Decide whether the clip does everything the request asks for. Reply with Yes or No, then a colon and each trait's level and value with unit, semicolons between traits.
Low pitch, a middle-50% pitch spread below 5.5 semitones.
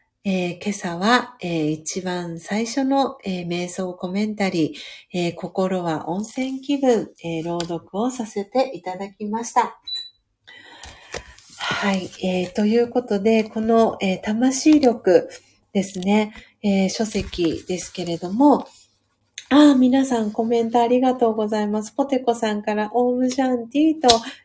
No: high, 215 Hz; average, 5.1 semitones